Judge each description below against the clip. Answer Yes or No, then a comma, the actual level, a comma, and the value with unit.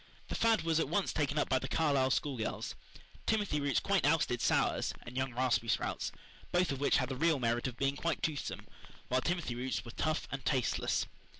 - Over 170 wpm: Yes, average, 200 wpm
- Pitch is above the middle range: No, medium, 140 Hz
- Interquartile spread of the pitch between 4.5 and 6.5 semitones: No, average, 4.0 semitones